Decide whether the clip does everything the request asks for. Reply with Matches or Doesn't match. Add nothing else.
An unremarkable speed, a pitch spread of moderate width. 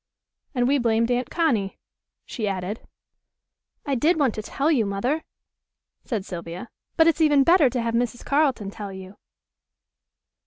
Doesn't match